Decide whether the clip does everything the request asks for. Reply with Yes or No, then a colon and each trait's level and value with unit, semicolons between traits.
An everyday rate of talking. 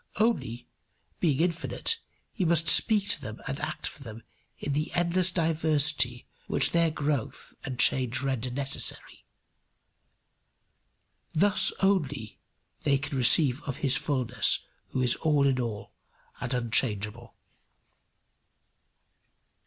No: slow, 115 wpm